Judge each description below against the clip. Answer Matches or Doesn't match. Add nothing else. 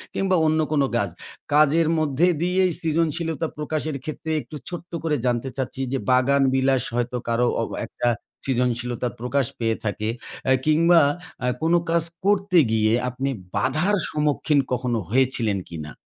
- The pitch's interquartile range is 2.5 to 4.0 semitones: Doesn't match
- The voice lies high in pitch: Doesn't match